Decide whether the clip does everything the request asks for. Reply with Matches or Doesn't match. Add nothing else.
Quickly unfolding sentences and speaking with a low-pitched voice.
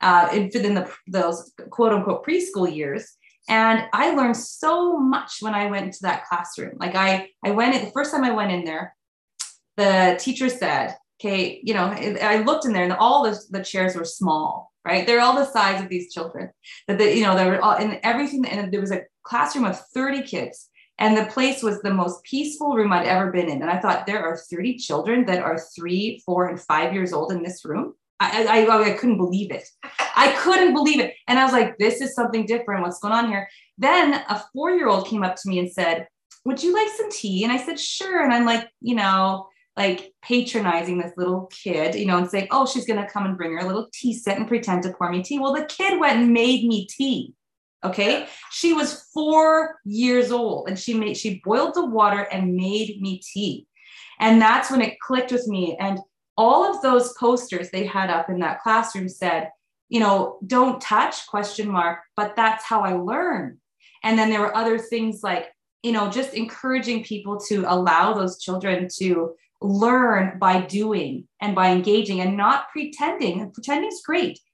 Doesn't match